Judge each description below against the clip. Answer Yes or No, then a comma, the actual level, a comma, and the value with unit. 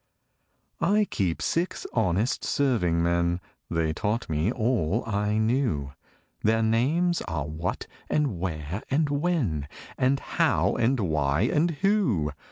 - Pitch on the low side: Yes, low, 110 Hz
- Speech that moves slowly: Yes, slow, 125 wpm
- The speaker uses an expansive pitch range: Yes, wide, 8.2 semitones